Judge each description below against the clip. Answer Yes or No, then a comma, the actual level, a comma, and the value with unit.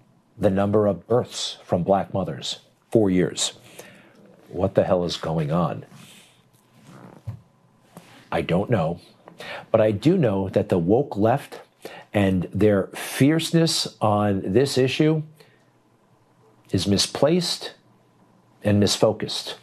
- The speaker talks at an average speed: No, slow, 110 wpm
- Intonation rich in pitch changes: Yes, wide, 6.7 semitones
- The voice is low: Yes, low, 105 Hz